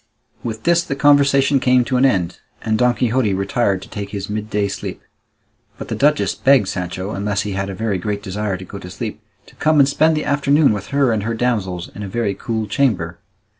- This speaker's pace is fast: Yes, fast, 215 wpm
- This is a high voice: No, low, 110 Hz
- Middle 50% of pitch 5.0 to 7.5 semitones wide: Yes, average, 5.3 semitones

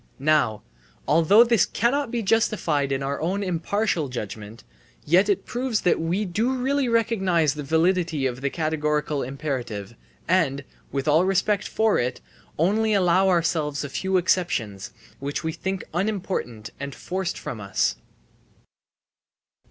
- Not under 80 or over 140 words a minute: Yes, slow, 135 wpm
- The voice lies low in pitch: No, medium, 170 Hz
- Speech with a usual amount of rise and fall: No, wide, 6.0 semitones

